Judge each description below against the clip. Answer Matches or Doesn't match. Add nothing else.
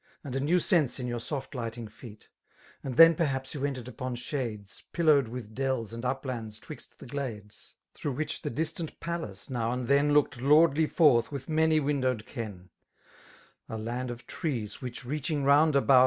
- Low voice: Matches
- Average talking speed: Matches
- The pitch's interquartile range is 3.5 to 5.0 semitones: Matches